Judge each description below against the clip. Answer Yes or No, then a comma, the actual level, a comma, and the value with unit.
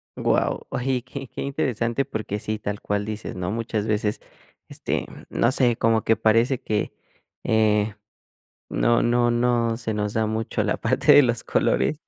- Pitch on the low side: Yes, low, 115 Hz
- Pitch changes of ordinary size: No, narrow, 2.1 semitones